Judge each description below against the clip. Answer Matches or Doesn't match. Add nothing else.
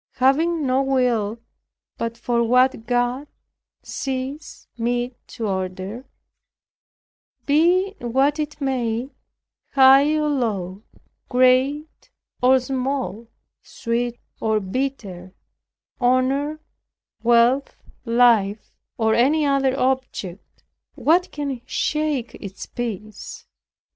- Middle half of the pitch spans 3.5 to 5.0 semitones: Doesn't match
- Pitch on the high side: Matches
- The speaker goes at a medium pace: Doesn't match